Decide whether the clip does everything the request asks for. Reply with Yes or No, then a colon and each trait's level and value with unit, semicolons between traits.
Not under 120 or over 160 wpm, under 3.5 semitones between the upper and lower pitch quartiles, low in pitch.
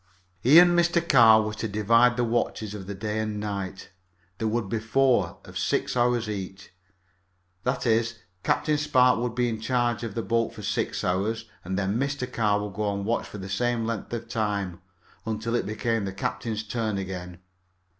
No: average, 190 wpm; average, 2.9 semitones; low, 110 Hz